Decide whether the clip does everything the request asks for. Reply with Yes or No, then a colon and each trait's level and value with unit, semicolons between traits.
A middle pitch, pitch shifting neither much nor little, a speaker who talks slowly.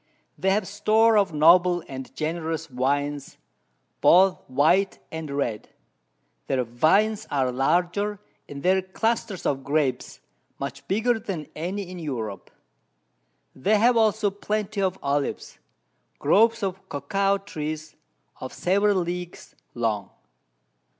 No: medium, 175 Hz; wide, 5.9 semitones; slow, 115 wpm